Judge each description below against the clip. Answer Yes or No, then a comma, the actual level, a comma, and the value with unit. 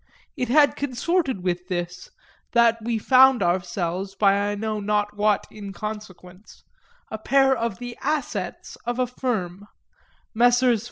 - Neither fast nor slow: No, slow, 130 wpm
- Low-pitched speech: No, high, 215 Hz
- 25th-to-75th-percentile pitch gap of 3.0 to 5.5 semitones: Yes, average, 4.1 semitones